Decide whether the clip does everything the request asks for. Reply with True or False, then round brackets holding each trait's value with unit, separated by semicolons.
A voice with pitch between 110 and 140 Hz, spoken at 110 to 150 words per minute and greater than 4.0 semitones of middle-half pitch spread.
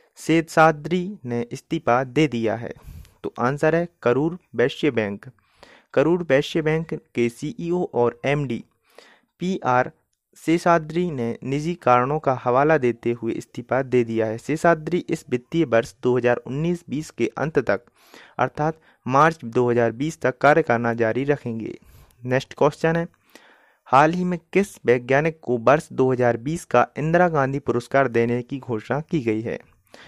True (135 Hz; 140 wpm; 5.1 semitones)